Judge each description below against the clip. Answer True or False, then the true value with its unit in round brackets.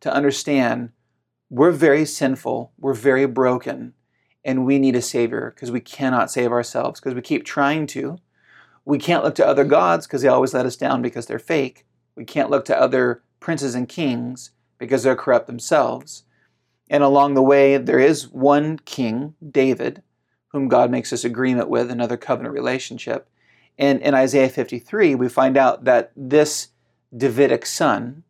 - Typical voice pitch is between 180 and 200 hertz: False (130 Hz)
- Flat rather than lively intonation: True (2.2 semitones)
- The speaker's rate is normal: True (170 wpm)